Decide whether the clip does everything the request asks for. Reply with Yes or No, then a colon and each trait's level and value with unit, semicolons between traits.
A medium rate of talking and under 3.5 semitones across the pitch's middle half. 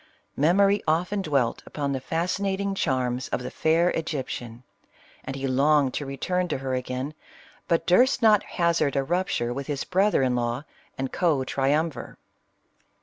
No: average, 150 wpm; average, 5.2 semitones